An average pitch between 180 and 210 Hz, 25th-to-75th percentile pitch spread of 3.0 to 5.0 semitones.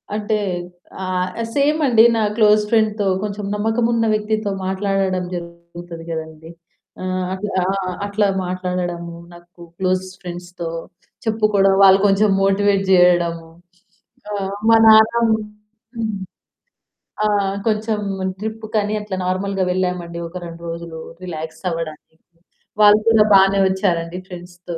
Yes: high, 190 Hz; average, 3.3 semitones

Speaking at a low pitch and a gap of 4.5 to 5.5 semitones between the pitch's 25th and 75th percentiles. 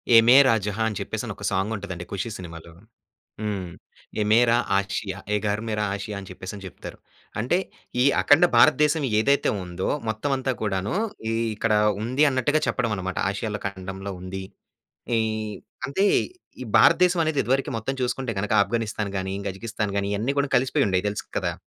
Yes: low, 110 Hz; average, 4.9 semitones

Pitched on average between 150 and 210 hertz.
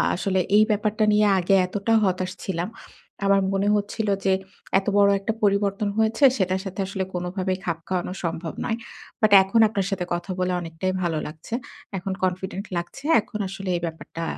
Yes: high, 190 Hz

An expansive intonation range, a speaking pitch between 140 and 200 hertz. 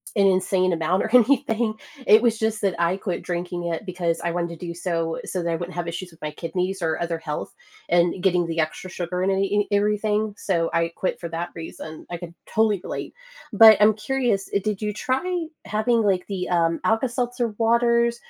No: average, 4.1 semitones; medium, 185 Hz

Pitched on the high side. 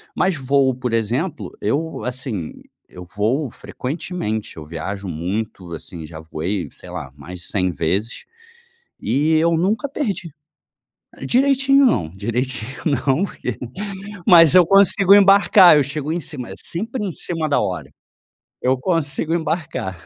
No: low, 135 Hz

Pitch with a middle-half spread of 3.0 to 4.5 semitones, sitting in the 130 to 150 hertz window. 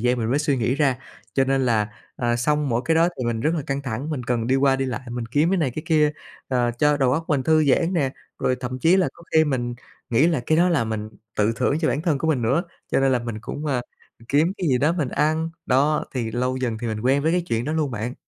Yes: average, 4.1 semitones; low, 135 Hz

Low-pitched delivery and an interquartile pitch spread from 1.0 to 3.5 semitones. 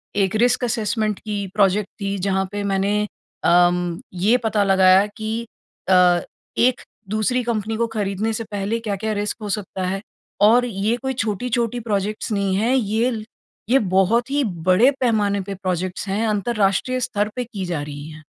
No: high, 210 Hz; average, 3.0 semitones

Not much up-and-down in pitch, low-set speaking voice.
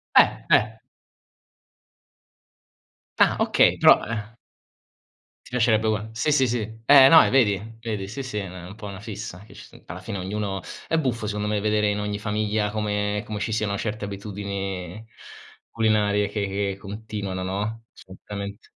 Yes: narrow, 1.7 semitones; low, 105 Hz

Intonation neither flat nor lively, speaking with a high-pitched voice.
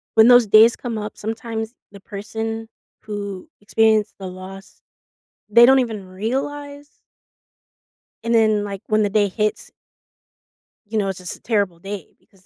No: narrow, 2.1 semitones; high, 215 Hz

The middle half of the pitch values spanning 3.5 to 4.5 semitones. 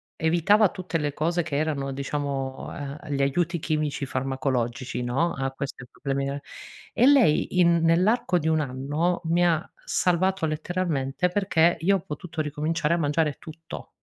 Yes: average, 3.8 semitones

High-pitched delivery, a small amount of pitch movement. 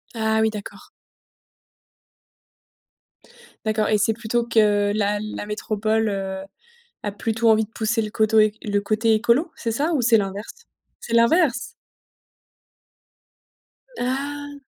Yes: high, 220 Hz; narrow, 1.9 semitones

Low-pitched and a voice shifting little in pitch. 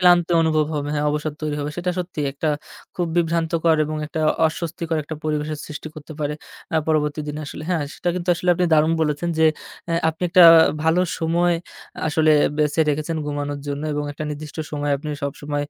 No: medium, 155 Hz; narrow, 2.1 semitones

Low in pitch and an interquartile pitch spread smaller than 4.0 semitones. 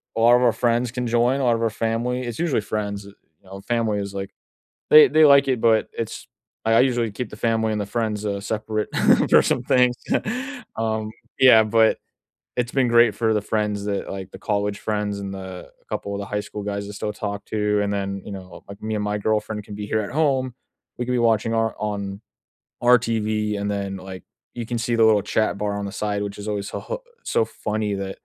Yes: low, 110 Hz; narrow, 2.4 semitones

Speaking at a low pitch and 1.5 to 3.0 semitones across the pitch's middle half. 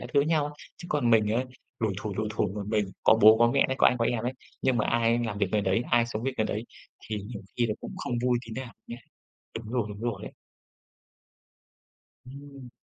Yes: low, 115 Hz; average, 2.7 semitones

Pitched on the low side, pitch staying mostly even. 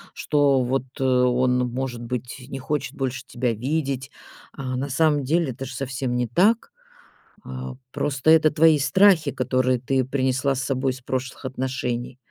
Yes: low, 130 Hz; narrow, 1.9 semitones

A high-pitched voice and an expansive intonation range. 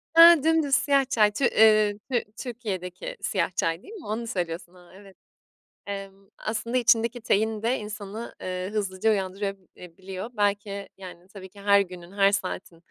No: high, 205 Hz; average, 3.3 semitones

